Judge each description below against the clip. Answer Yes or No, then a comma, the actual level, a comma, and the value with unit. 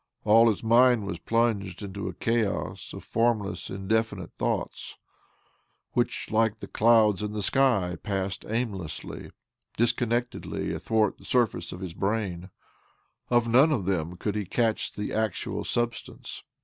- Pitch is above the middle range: No, low, 110 Hz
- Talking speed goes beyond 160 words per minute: No, average, 140 wpm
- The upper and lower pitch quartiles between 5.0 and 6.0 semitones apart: No, average, 3.1 semitones